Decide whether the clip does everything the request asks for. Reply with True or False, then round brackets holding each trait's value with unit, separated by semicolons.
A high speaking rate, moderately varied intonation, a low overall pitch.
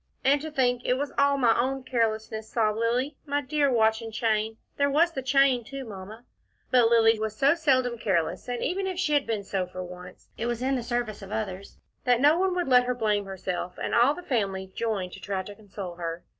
False (225 wpm; 4.4 semitones; 235 Hz)